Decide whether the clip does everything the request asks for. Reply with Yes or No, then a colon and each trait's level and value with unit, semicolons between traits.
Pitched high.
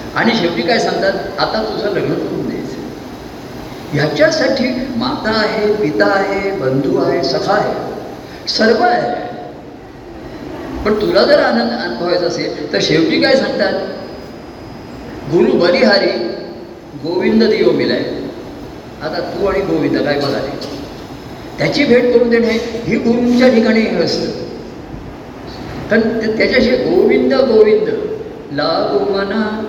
Yes: high, 230 Hz